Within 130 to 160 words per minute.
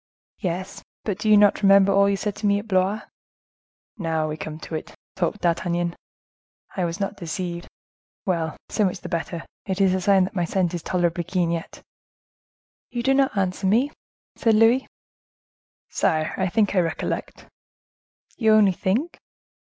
No: average, 170 wpm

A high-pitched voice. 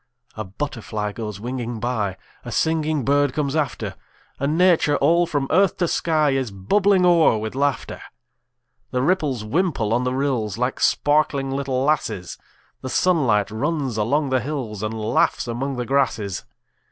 No: low, 135 Hz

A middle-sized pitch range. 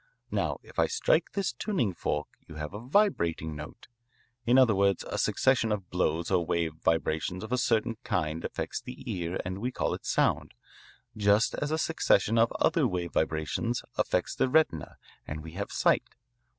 No: wide, 7.0 semitones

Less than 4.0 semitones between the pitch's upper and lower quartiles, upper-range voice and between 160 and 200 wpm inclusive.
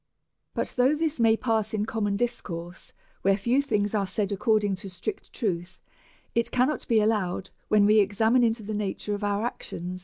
Yes: average, 2.7 semitones; high, 210 Hz; average, 185 wpm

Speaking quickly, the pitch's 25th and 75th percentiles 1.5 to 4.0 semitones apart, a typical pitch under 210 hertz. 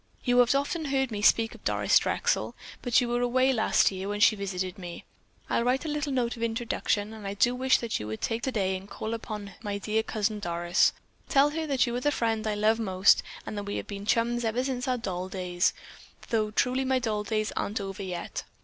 No: fast, 230 wpm; average, 3.5 semitones; high, 220 Hz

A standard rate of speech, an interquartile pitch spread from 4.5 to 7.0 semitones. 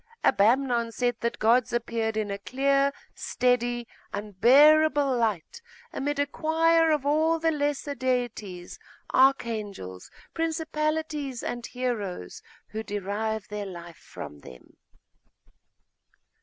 No: slow, 105 wpm; average, 5.2 semitones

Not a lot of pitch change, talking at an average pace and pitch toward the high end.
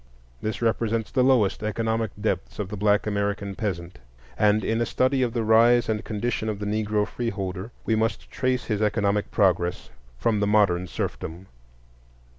No: narrow, 2.0 semitones; average, 165 wpm; low, 105 Hz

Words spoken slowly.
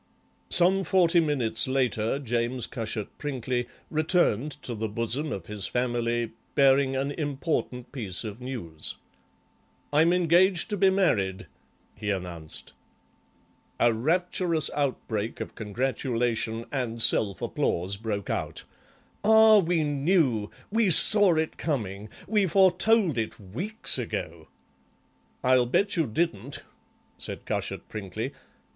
Yes: slow, 115 wpm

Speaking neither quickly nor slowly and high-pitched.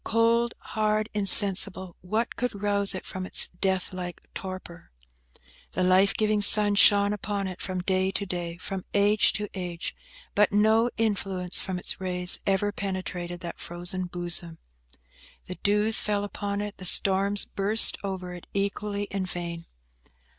Yes: average, 150 wpm; high, 195 Hz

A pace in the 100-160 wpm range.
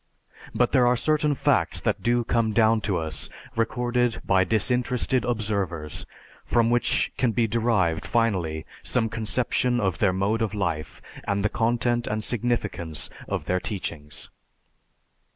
Yes: average, 140 wpm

